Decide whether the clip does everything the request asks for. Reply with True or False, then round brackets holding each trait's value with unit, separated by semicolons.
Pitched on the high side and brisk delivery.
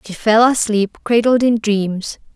False (220 Hz; 155 wpm)